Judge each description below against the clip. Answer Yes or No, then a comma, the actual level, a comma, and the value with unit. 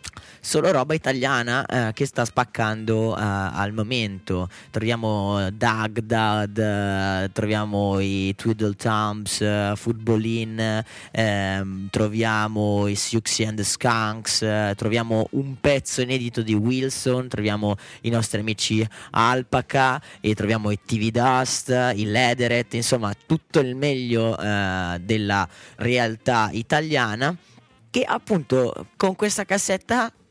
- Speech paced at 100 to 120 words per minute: Yes, slow, 115 wpm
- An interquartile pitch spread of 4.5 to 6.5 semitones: No, average, 3.3 semitones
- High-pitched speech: No, low, 110 Hz